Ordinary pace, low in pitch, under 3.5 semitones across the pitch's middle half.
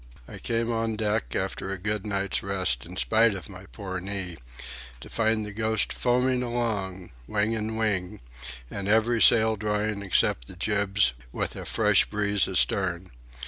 Yes: average, 160 wpm; low, 105 Hz; average, 2.7 semitones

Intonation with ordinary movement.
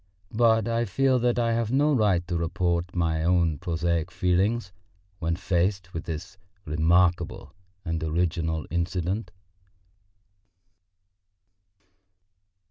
Yes: average, 4.2 semitones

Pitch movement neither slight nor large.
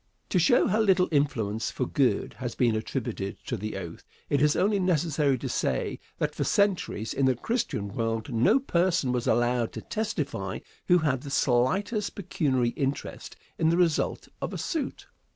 No: wide, 7.4 semitones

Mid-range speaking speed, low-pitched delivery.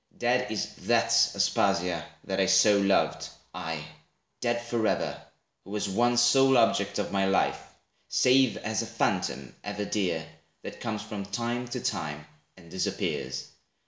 Yes: average, 145 wpm; low, 105 Hz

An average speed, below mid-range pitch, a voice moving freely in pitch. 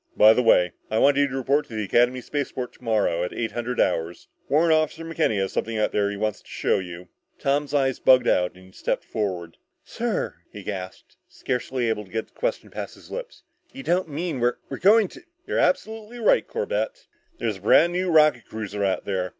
No: fast, 215 wpm; low, 125 Hz; wide, 7.7 semitones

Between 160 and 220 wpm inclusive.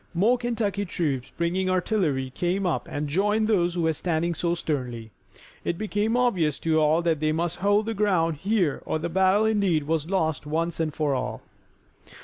Yes: average, 180 wpm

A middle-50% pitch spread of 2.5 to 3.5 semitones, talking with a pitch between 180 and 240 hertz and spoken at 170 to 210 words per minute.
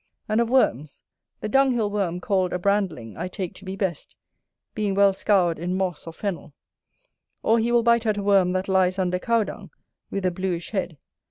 Yes: average, 2.8 semitones; high, 190 Hz; average, 195 wpm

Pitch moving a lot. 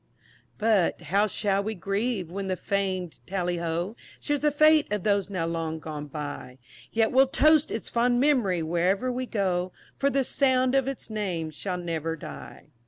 Yes: wide, 6.3 semitones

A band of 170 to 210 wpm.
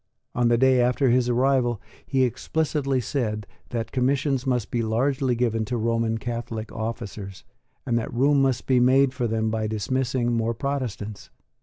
No: average, 160 wpm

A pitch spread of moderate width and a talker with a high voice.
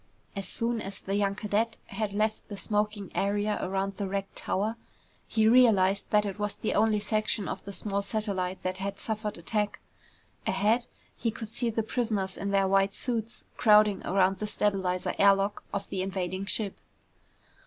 No: narrow, 1.7 semitones; high, 205 Hz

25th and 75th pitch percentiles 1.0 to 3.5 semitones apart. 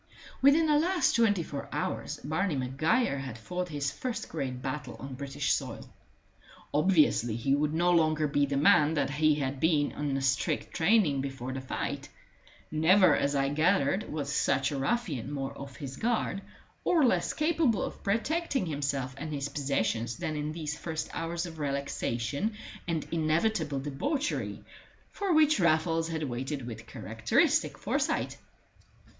No: average, 4.7 semitones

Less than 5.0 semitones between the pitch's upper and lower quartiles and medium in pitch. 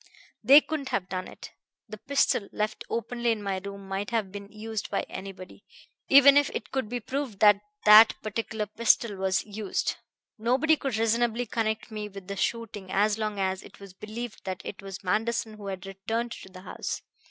No: average, 2.9 semitones; high, 215 Hz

